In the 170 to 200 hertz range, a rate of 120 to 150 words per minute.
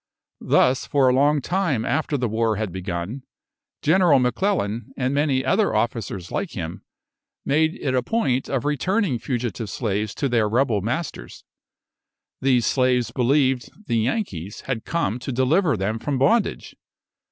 No: low, 130 Hz; average, 145 wpm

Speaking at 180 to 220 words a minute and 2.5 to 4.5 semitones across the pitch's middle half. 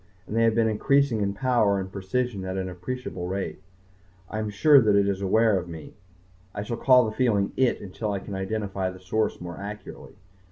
Yes: fast, 205 wpm; average, 3.2 semitones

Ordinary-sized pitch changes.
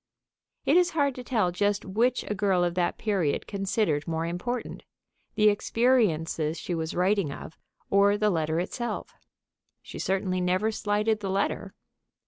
Yes: average, 3.6 semitones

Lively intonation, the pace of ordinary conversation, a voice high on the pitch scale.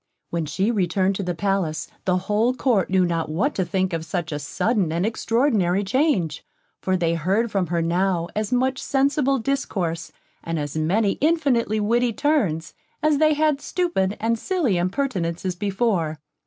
Yes: wide, 6.3 semitones; average, 165 wpm; high, 195 Hz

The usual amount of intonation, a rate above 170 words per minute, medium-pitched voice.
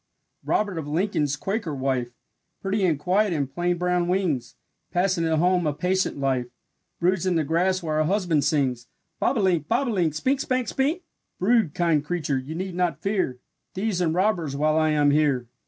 Yes: average, 4.2 semitones; average, 180 wpm; medium, 170 Hz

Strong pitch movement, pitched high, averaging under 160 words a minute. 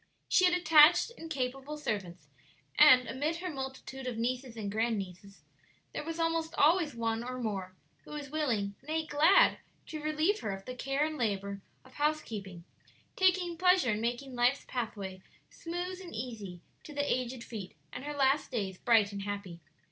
No: wide, 6.4 semitones; very high, 255 Hz; average, 170 wpm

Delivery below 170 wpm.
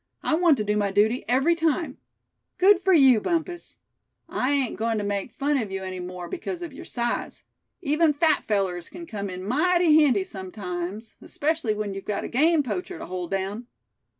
No: average, 190 wpm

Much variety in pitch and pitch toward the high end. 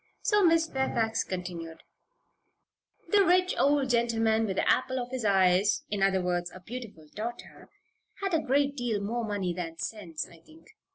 Yes: wide, 6.3 semitones; high, 225 Hz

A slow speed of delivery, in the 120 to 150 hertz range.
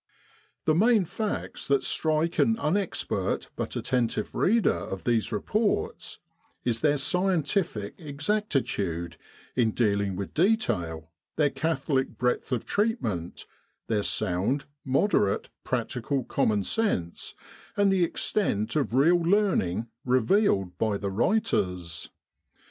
Yes: slow, 110 wpm; low, 135 Hz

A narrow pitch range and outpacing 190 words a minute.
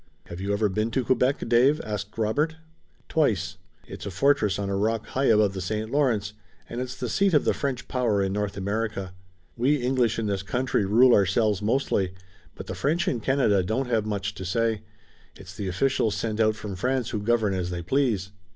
No: average, 4.1 semitones; fast, 205 wpm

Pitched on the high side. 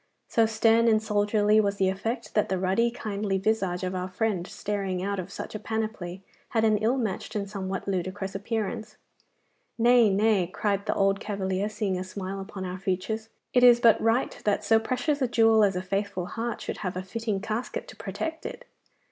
Yes: high, 205 Hz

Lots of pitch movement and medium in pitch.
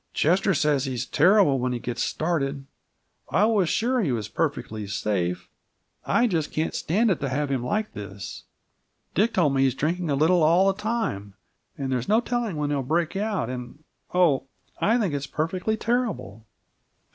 Yes: wide, 7.1 semitones; medium, 155 Hz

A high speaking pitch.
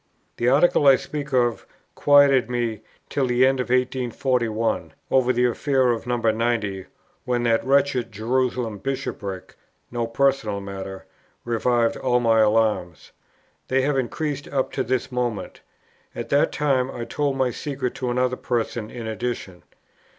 No: low, 125 Hz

